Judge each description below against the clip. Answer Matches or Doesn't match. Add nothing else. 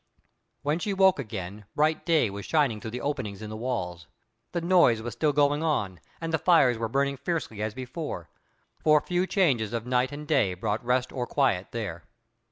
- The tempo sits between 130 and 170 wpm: Doesn't match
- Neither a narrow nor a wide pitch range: Doesn't match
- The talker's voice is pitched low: Matches